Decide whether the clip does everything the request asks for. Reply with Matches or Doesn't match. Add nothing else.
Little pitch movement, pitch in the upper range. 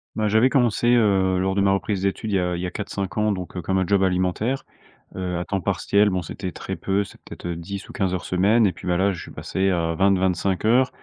Doesn't match